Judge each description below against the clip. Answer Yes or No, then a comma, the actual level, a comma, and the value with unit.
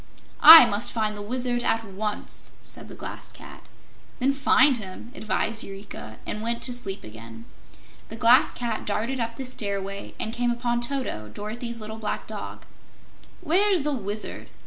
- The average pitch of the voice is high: Yes, high, 230 Hz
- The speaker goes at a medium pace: Yes, average, 160 wpm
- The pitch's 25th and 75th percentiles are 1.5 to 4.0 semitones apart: Yes, average, 3.1 semitones